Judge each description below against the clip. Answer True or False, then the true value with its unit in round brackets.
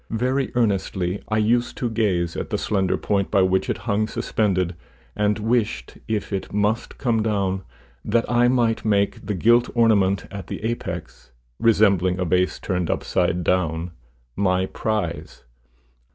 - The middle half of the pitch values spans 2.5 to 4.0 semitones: True (3.4 semitones)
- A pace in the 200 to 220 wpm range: False (150 wpm)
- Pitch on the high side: False (100 Hz)